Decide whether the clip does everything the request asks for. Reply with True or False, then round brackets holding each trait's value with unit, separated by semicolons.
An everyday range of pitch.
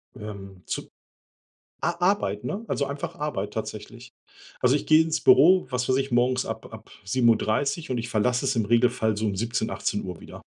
True (4.7 semitones)